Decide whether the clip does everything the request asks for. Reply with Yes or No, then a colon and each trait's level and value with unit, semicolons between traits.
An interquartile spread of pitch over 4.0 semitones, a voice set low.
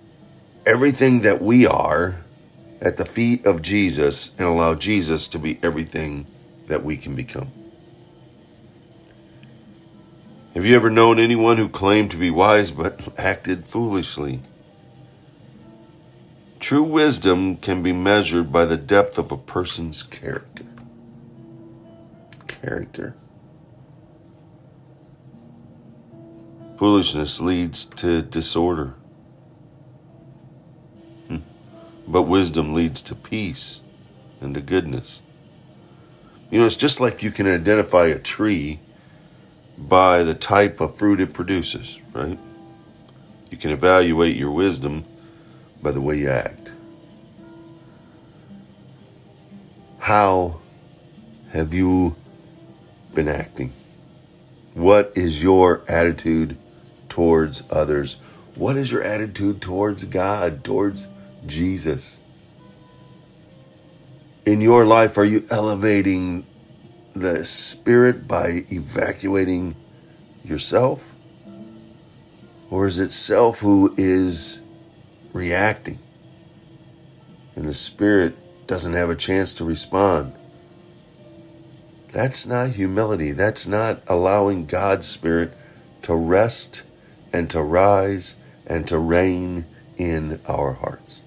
Yes: average, 4.7 semitones; very low, 95 Hz